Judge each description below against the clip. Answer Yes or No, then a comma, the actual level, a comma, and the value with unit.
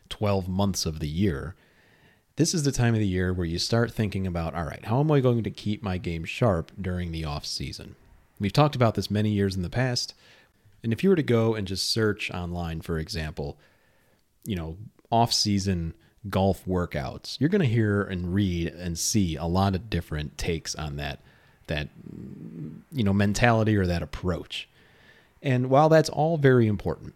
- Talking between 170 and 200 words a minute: Yes, average, 190 wpm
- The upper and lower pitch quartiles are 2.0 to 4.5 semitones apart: No, average, 5.0 semitones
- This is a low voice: Yes, low, 100 Hz